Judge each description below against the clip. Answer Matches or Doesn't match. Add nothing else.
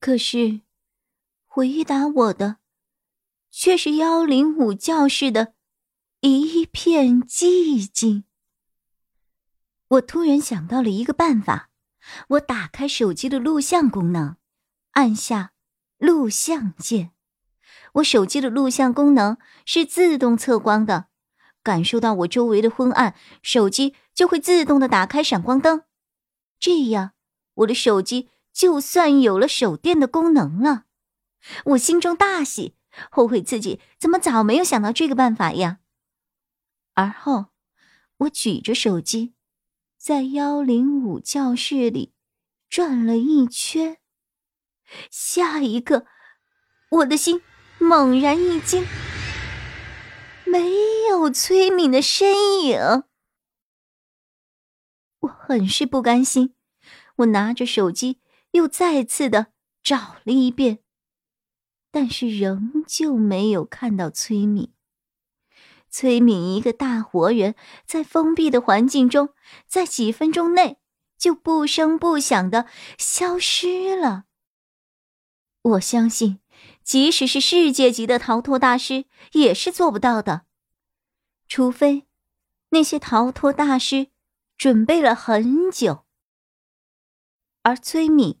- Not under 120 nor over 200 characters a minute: Matches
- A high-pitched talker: Matches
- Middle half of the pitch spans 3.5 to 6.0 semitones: Matches